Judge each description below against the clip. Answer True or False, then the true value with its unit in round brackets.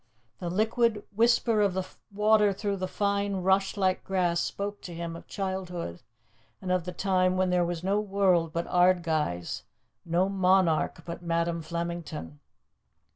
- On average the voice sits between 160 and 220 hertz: True (185 Hz)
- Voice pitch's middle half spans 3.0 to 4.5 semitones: False (2.6 semitones)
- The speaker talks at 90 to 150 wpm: True (145 wpm)